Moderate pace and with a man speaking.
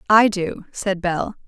No: average, 165 wpm; female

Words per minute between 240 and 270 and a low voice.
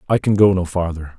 Yes: fast, 255 wpm; very low, 90 Hz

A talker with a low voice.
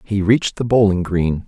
Yes: low, 100 Hz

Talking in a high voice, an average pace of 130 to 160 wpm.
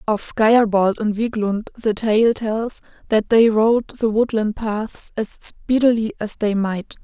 Yes: high, 220 Hz; average, 155 wpm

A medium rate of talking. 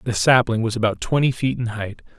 No: fast, 220 wpm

